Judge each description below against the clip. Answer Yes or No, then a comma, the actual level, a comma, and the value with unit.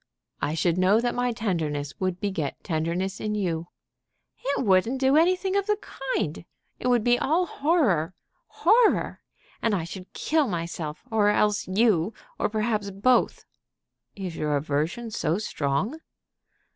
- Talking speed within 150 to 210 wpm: No, average, 140 wpm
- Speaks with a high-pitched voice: Yes, high, 205 Hz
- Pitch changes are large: Yes, wide, 6.5 semitones